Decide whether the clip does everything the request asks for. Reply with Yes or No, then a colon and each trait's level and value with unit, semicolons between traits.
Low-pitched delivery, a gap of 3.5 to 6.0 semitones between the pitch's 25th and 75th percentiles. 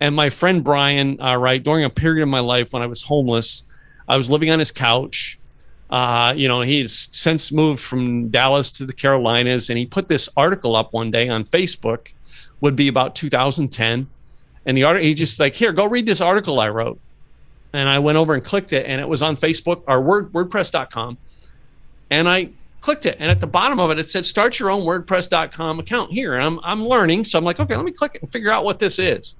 No: medium, 145 Hz; average, 5.3 semitones